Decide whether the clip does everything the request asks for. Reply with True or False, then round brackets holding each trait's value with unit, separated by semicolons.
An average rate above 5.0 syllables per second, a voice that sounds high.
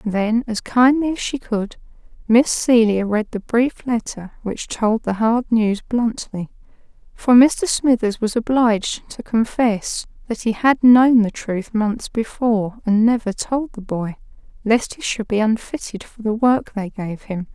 False (4.0 syllables/s; 225 Hz)